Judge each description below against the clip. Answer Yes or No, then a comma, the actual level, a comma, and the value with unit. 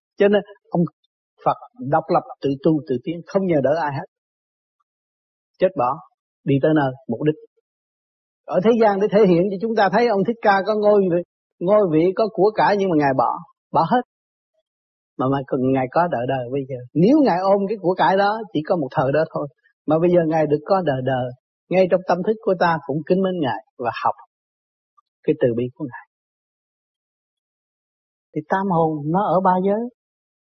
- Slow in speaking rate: No, average, 200 wpm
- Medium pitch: Yes, medium, 175 Hz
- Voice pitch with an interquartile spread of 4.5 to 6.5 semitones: Yes, average, 5.2 semitones